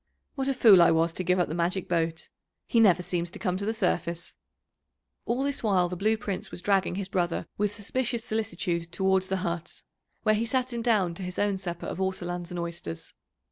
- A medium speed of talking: No, fast, 215 wpm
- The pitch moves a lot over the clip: No, average, 3.8 semitones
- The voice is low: No, medium, 185 Hz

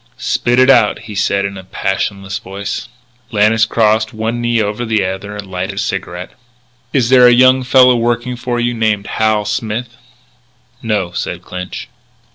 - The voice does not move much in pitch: No, average, 3.4 semitones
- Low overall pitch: Yes, low, 110 Hz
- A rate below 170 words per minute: Yes, average, 160 wpm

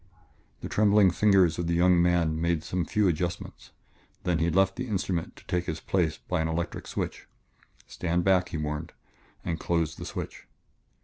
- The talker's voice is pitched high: No, very low, 85 Hz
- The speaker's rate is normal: Yes, average, 175 wpm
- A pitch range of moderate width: No, narrow, 2.1 semitones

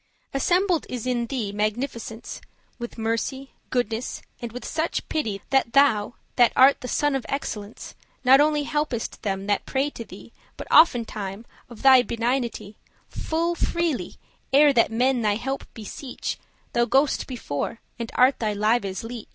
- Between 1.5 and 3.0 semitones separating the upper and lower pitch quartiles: No, average, 3.5 semitones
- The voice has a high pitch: Yes, high, 245 Hz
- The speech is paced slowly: No, average, 155 wpm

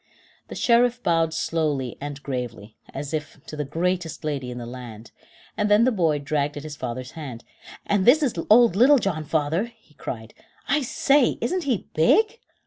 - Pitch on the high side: No, medium, 160 Hz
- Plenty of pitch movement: Yes, wide, 8.5 semitones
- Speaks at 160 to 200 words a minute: Yes, average, 180 wpm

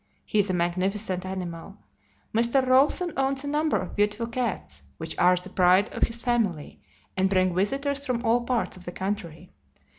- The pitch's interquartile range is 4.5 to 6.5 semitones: Yes, average, 5.3 semitones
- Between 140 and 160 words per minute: No, average, 175 wpm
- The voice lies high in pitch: Yes, high, 205 Hz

